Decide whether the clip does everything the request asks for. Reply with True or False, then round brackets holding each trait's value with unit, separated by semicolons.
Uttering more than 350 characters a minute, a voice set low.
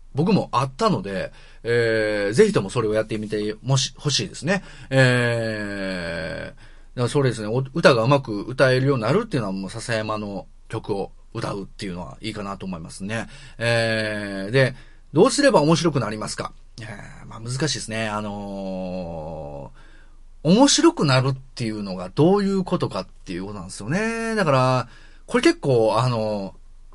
False (335 characters per minute; 115 Hz)